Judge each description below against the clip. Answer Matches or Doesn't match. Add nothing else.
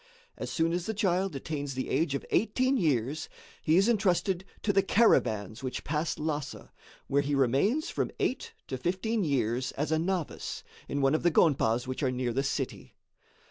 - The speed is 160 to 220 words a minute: Matches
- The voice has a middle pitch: Matches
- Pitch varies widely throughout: Matches